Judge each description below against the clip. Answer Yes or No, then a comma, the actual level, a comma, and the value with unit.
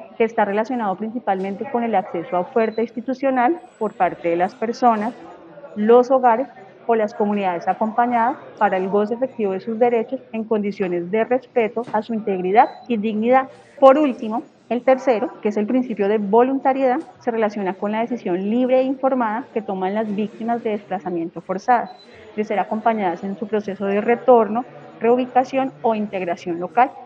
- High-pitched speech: Yes, high, 225 Hz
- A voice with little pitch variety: No, average, 3.2 semitones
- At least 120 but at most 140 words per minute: No, average, 165 wpm